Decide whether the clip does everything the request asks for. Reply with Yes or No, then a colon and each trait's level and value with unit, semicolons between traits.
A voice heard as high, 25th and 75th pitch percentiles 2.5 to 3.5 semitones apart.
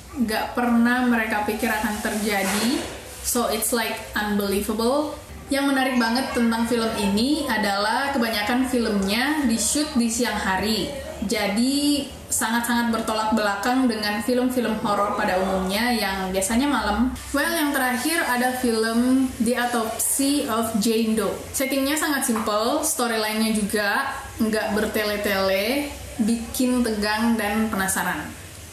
Yes: high, 230 Hz; average, 3.1 semitones